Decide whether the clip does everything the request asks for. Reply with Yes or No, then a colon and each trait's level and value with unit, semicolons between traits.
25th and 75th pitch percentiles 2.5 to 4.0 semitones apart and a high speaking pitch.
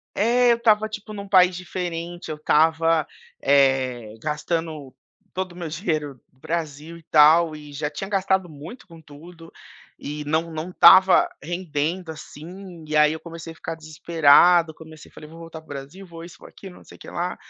No: average, 2.8 semitones; medium, 165 Hz